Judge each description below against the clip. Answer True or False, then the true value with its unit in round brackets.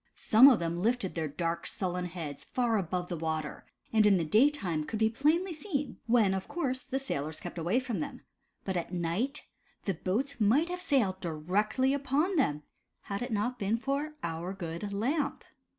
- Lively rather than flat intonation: True (7.4 semitones)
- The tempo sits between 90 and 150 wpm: False (180 wpm)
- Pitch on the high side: True (210 Hz)